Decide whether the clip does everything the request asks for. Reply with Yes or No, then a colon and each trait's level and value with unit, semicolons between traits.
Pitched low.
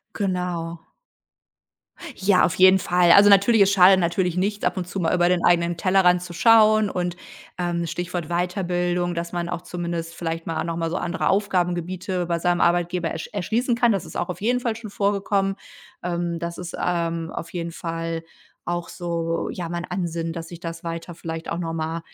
No: medium, 175 Hz